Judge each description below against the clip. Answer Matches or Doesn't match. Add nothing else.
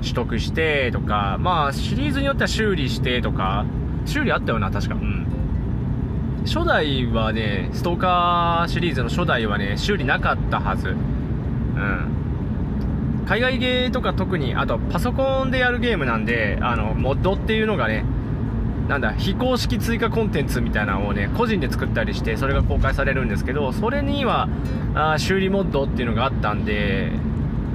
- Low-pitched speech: Matches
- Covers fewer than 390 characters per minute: Matches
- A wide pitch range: Doesn't match